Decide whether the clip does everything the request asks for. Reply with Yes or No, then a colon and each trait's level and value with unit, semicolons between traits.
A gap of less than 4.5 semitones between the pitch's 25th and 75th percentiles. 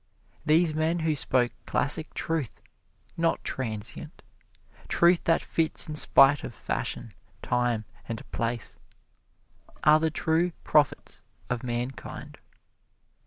No: average, 4.8 semitones